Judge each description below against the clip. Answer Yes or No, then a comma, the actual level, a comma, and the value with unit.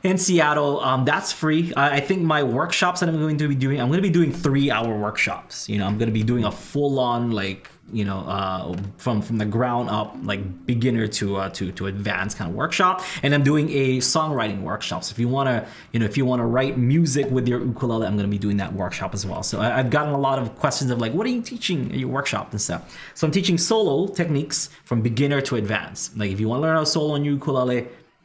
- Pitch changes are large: Yes, wide, 5.9 semitones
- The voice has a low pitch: Yes, low, 125 Hz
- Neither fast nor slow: No, fast, 245 wpm